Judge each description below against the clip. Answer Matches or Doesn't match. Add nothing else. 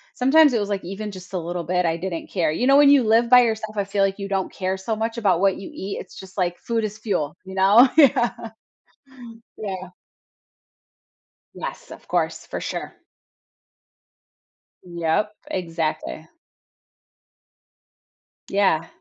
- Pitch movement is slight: Doesn't match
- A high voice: Matches